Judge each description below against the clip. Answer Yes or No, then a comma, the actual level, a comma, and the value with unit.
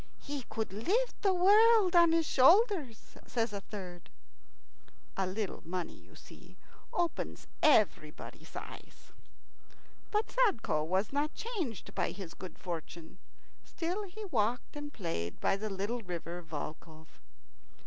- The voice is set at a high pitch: Yes, high, 225 Hz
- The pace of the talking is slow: Yes, slow, 130 wpm